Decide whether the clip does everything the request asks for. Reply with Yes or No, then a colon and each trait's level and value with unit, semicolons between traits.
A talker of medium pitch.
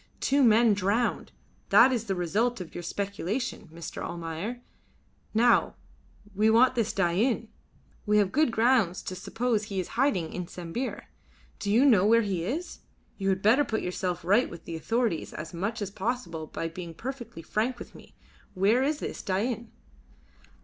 No: high, 210 Hz